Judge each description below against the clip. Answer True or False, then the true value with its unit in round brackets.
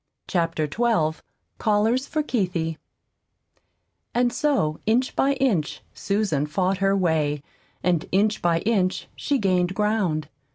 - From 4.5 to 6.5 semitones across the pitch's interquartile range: True (5.5 semitones)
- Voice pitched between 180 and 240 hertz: True (190 Hz)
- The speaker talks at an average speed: False (120 wpm)